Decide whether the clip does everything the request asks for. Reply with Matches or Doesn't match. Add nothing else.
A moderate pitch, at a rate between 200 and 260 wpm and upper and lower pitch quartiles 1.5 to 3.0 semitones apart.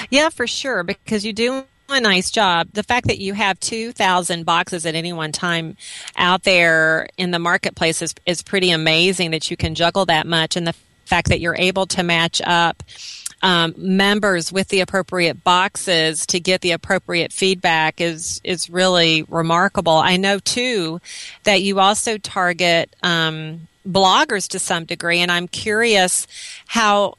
Doesn't match